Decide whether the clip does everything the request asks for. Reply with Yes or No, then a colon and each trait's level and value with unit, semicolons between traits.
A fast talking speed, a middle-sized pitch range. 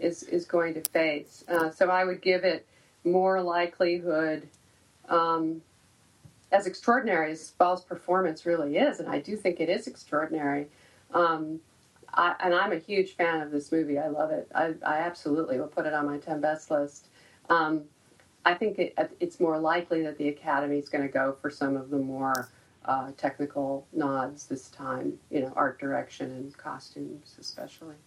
No: average, 175 wpm; average, 3.1 semitones